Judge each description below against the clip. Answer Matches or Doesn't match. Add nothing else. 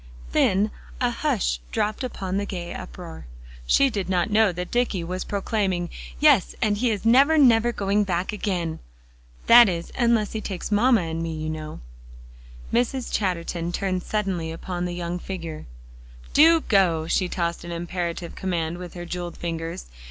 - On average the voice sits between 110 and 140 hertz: Doesn't match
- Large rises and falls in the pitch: Doesn't match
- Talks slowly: Doesn't match